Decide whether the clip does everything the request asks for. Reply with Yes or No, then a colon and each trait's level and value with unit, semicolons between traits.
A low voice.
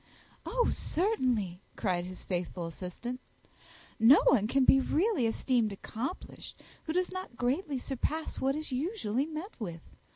No: very high, 255 Hz